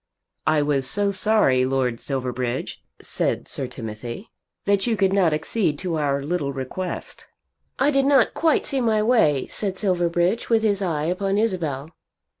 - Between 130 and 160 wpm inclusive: Yes, average, 155 wpm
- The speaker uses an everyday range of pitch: No, wide, 6.9 semitones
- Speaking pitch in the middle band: Yes, medium, 175 Hz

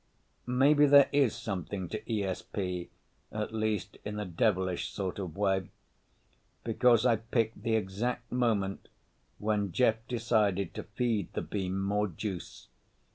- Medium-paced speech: No, slow, 125 wpm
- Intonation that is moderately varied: Yes, average, 3.2 semitones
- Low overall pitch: Yes, low, 105 Hz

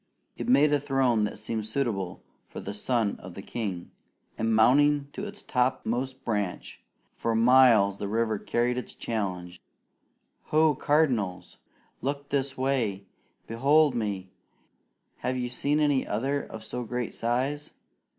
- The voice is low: Yes, low, 120 Hz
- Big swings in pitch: No, average, 4.5 semitones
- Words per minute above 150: No, average, 140 wpm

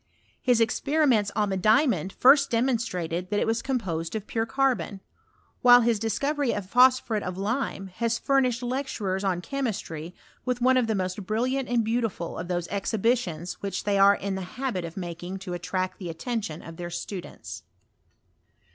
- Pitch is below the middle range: No, high, 215 Hz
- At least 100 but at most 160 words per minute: No, average, 170 wpm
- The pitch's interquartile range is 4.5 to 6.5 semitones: Yes, average, 5.0 semitones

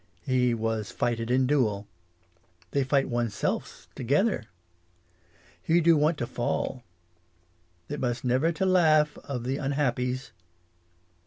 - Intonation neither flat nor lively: Yes, average, 3.7 semitones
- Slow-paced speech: Yes, slow, 120 wpm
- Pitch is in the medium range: No, low, 130 Hz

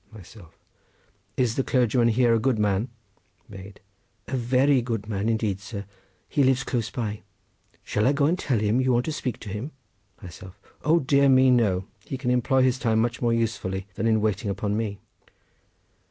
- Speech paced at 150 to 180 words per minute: Yes, average, 170 wpm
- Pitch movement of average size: Yes, average, 3.8 semitones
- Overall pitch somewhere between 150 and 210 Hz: No, low, 115 Hz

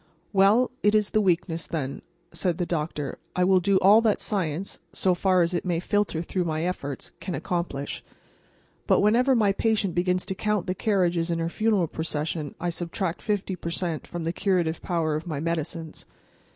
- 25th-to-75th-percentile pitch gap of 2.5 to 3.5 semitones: Yes, average, 3.1 semitones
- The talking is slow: No, average, 180 wpm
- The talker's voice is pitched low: No, medium, 175 Hz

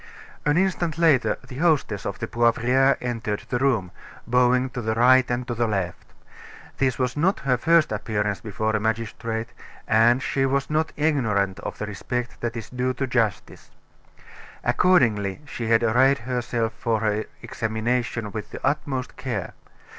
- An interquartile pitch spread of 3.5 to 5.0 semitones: No, average, 3.0 semitones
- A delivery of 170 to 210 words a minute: No, average, 160 wpm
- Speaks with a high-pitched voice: No, low, 120 Hz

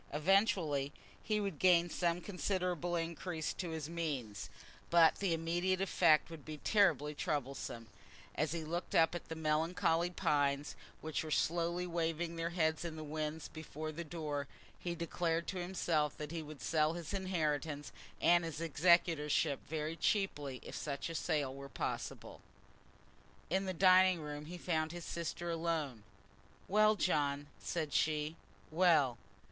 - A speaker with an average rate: Yes, average, 150 wpm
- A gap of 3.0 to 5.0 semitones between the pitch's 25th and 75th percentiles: No, narrow, 2.5 semitones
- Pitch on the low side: No, medium, 165 Hz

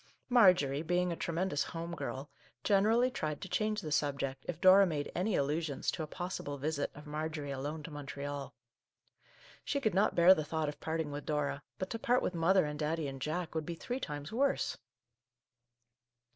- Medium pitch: Yes, medium, 160 Hz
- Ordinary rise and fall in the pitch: Yes, average, 4.2 semitones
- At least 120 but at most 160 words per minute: No, average, 185 wpm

